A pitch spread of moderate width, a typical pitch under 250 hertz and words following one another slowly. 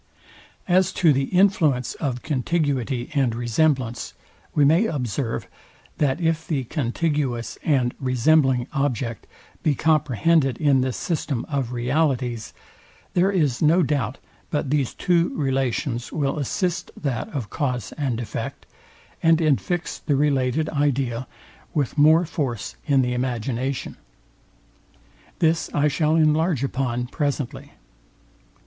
Yes: average, 4.0 semitones; medium, 140 Hz; slow, 120 wpm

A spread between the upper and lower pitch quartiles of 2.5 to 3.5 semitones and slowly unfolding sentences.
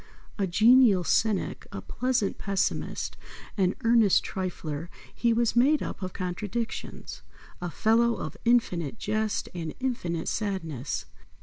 No: average, 4.7 semitones; slow, 120 wpm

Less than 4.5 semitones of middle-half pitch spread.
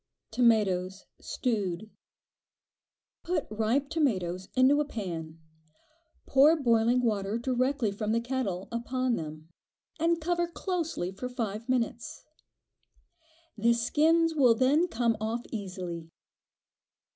No: average, 5.3 semitones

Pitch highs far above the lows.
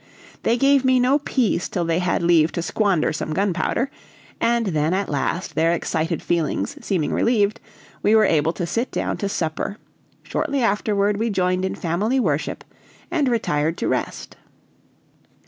Yes: wide, 5.7 semitones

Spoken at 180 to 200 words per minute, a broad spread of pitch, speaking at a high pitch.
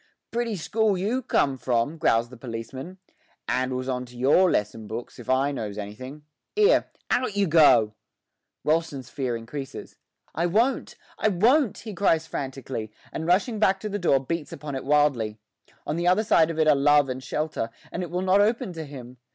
No: average, 185 wpm; wide, 6.5 semitones; medium, 150 Hz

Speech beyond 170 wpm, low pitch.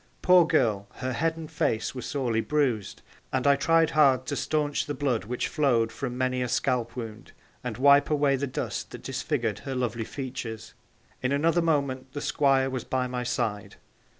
Yes: average, 180 wpm; low, 130 Hz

